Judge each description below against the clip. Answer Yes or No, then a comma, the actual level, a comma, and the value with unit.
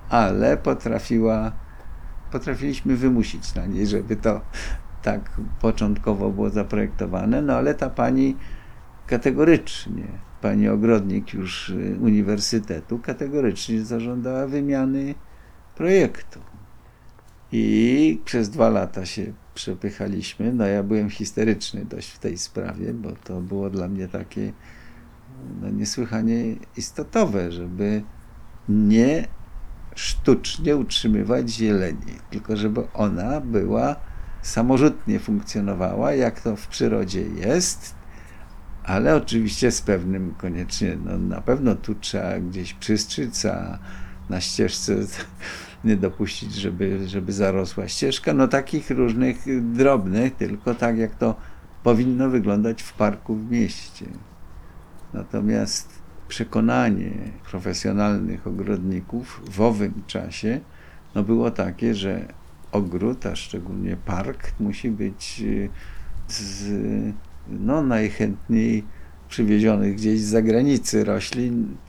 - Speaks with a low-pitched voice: Yes, low, 105 Hz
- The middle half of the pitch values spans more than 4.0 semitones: No, average, 3.7 semitones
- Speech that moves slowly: Yes, slow, 105 wpm